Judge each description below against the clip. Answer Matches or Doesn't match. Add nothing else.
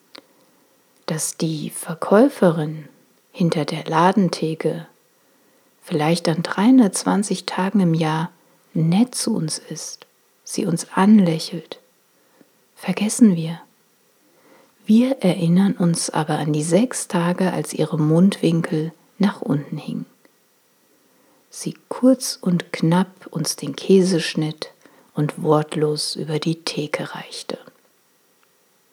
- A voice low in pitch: Doesn't match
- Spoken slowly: Matches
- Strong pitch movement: Doesn't match